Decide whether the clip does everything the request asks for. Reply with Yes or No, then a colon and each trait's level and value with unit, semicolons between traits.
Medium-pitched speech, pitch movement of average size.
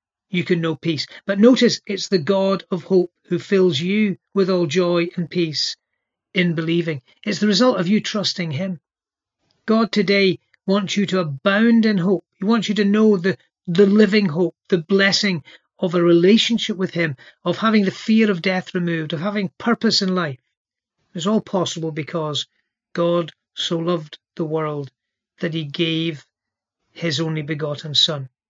Yes: medium, 180 Hz; average, 3.4 semitones